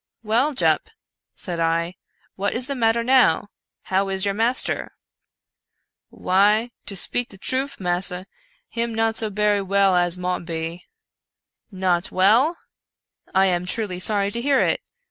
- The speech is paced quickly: No, average, 165 wpm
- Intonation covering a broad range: No, average, 4.1 semitones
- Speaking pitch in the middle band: No, high, 200 Hz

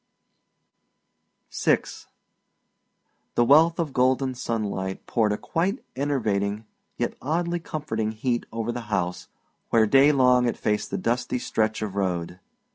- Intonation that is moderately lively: Yes, average, 4.4 semitones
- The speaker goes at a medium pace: No, slow, 125 wpm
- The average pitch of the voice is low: Yes, low, 120 Hz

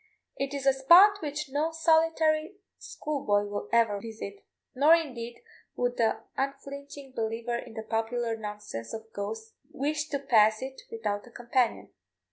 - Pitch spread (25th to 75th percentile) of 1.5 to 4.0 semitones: No, average, 4.8 semitones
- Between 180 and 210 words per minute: No, average, 145 wpm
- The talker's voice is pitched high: Yes, very high, 250 Hz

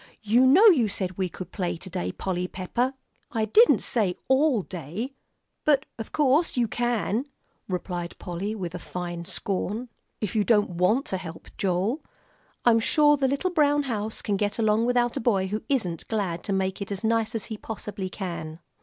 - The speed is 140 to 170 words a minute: No, average, 185 wpm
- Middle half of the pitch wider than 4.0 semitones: Yes, average, 4.9 semitones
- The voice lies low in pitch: No, high, 210 Hz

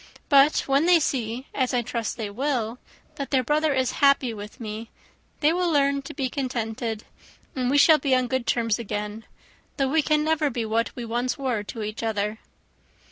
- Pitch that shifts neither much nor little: Yes, average, 3.8 semitones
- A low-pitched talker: No, very high, 255 Hz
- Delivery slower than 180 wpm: No, average, 190 wpm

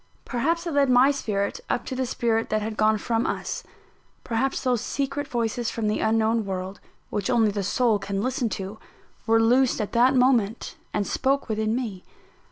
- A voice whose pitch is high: Yes, high, 225 Hz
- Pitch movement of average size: Yes, average, 3.2 semitones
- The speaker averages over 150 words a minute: Yes, average, 180 wpm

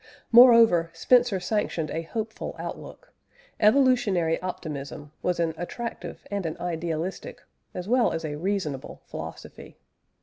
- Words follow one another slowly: Yes, slow, 115 wpm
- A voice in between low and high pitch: Yes, medium, 180 Hz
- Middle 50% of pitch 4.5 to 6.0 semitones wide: Yes, wide, 5.5 semitones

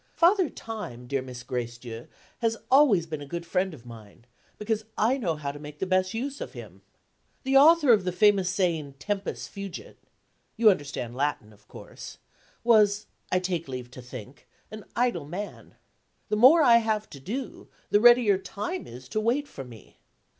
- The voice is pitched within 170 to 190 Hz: Yes, medium, 185 Hz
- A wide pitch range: Yes, wide, 8.6 semitones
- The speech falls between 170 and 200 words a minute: Yes, average, 175 wpm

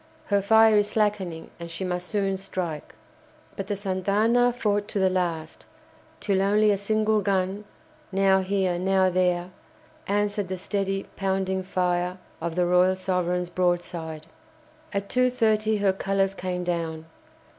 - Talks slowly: No, average, 145 wpm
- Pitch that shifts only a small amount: Yes, narrow, 2.3 semitones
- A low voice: No, high, 190 Hz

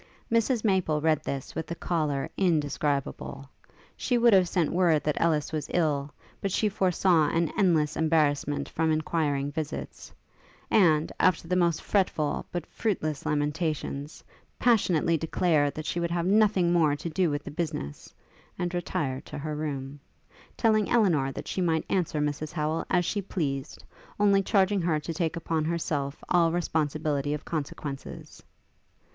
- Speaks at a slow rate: No, average, 150 wpm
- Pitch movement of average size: Yes, average, 3.2 semitones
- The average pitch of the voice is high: No, medium, 160 Hz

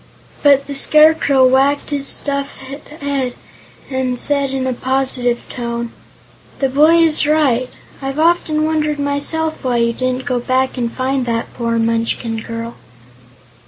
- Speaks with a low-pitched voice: No, very high, 270 Hz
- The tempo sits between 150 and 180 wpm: No, average, 140 wpm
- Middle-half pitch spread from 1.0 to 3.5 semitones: Yes, average, 2.7 semitones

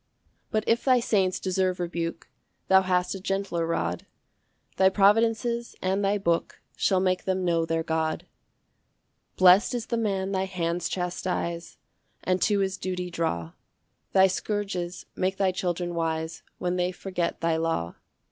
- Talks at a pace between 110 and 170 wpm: Yes, average, 155 wpm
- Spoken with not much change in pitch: Yes, narrow, 2.3 semitones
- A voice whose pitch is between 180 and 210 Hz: Yes, medium, 185 Hz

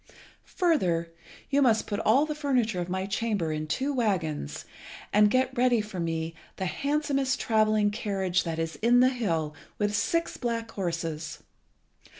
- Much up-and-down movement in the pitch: Yes, wide, 6.7 semitones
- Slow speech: No, average, 155 wpm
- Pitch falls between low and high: No, high, 210 Hz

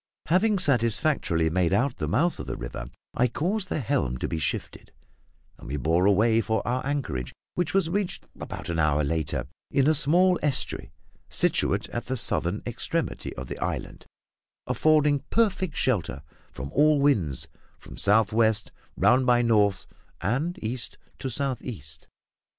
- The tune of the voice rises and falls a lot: Yes, wide, 8.9 semitones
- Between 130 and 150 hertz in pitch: No, low, 120 Hz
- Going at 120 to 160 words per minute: Yes, average, 155 wpm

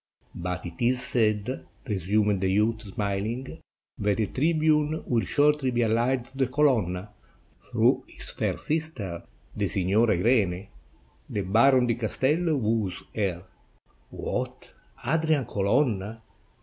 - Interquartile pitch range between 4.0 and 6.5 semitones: Yes, average, 4.9 semitones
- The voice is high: No, low, 115 Hz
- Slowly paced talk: Yes, slow, 125 wpm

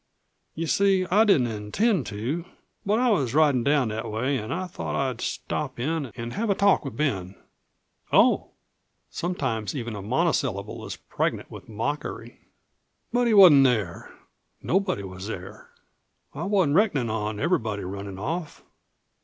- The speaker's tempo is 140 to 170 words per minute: Yes, average, 150 wpm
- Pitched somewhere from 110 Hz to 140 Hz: Yes, low, 135 Hz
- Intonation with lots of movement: Yes, wide, 8.5 semitones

